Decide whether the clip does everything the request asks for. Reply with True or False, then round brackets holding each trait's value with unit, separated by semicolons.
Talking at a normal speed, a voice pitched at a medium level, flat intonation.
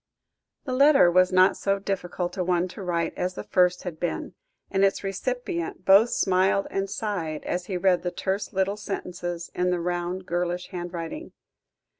True (170 wpm; 180 Hz; 1.9 semitones)